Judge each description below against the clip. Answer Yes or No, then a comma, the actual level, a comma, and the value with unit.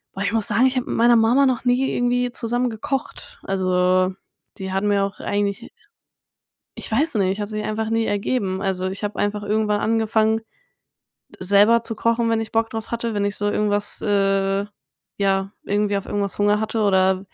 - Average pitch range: No, narrow, 2.3 semitones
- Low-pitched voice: No, high, 210 Hz